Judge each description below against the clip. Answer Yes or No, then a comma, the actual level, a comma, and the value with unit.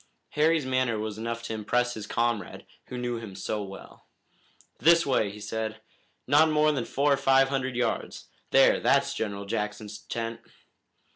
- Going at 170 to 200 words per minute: No, average, 160 wpm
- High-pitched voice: No, low, 115 Hz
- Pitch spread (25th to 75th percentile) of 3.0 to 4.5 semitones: Yes, average, 3.8 semitones